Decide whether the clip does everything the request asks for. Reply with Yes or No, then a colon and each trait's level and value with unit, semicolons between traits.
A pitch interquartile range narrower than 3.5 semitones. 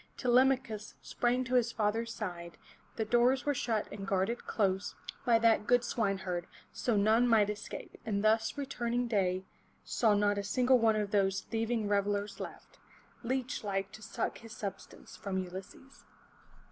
Yes: average, 3.1 semitones